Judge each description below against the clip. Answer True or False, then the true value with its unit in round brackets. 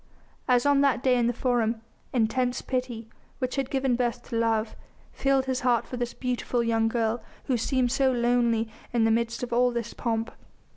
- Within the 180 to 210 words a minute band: True (190 wpm)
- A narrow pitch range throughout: True (1.7 semitones)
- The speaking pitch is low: False (245 Hz)